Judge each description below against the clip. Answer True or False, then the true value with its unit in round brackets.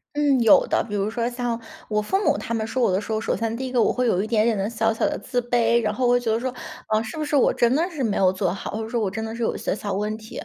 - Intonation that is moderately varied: False (2.3 semitones)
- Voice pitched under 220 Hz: False (225 Hz)